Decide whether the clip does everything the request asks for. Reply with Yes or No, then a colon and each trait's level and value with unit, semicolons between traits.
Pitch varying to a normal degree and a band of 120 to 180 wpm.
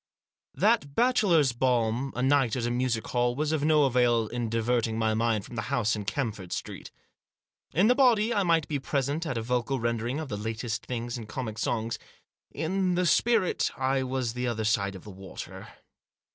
No: average, 4.6 semitones; average, 190 wpm